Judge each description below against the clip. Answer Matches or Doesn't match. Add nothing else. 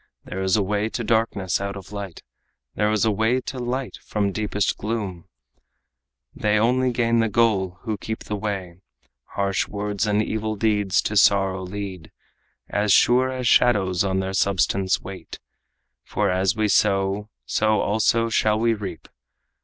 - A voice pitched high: Doesn't match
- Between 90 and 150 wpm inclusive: Doesn't match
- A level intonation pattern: Matches